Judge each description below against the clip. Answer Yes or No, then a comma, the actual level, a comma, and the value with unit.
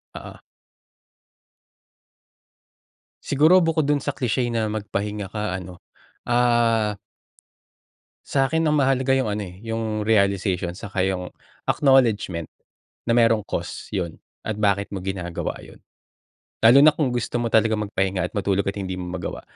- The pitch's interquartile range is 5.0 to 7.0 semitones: No, average, 4.1 semitones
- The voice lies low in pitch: Yes, low, 105 Hz